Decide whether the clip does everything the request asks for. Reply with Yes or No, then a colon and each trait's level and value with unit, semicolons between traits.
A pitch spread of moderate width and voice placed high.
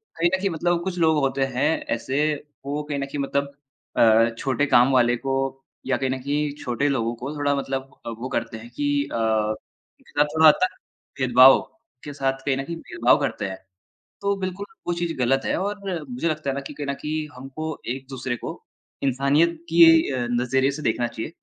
No: average, 3.4 semitones; low, 135 Hz